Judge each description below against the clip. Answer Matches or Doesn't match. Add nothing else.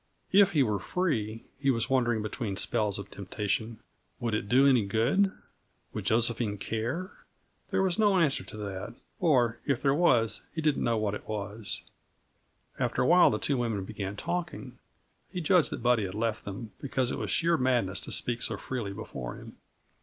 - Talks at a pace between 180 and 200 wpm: Matches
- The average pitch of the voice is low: Matches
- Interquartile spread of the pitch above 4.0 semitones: Matches